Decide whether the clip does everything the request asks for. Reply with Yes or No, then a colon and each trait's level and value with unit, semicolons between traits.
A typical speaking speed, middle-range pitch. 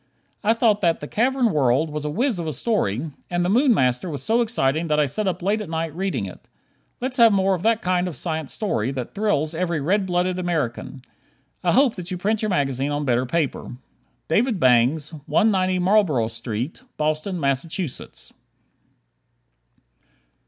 Yes: average, 175 wpm; medium, 170 Hz